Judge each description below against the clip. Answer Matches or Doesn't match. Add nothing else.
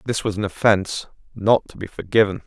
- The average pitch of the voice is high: Doesn't match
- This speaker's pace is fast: Doesn't match